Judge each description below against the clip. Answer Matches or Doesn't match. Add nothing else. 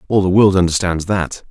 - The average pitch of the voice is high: Doesn't match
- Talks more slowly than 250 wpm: Matches